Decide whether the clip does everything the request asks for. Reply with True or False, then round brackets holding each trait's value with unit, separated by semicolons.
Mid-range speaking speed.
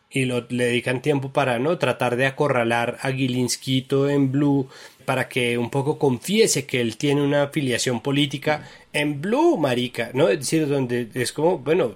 True (175 wpm)